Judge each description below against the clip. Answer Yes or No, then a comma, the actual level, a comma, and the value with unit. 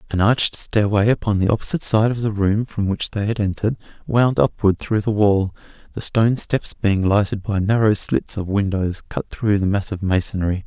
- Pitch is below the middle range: Yes, low, 105 Hz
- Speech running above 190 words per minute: Yes, average, 200 wpm